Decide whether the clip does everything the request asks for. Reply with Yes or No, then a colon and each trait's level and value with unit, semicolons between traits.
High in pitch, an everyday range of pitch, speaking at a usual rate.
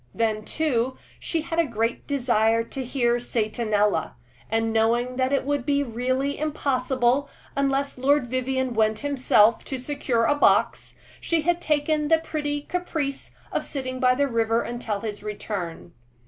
Yes: very high, 255 Hz; average, 3.9 semitones; average, 150 wpm